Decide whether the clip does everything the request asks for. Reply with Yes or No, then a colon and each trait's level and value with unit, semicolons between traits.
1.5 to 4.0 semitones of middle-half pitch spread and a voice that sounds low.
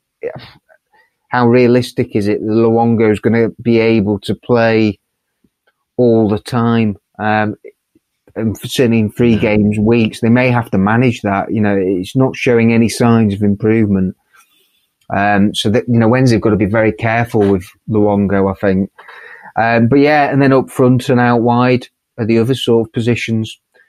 Yes: narrow, 2.5 semitones; low, 115 Hz